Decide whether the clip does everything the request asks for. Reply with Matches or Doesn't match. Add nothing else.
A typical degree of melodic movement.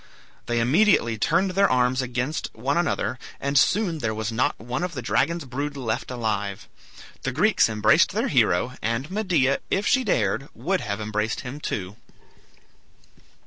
Doesn't match